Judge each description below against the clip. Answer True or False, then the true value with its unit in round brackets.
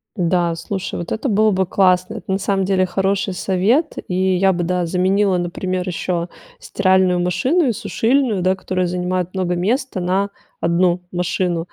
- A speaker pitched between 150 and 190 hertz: True (185 Hz)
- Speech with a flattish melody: True (1.7 semitones)